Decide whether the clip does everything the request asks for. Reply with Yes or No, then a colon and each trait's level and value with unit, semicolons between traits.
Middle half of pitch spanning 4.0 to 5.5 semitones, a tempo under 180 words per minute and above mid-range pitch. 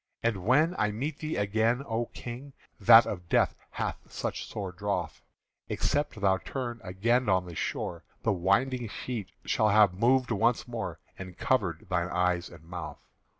No: average, 4.9 semitones; average, 160 wpm; low, 105 Hz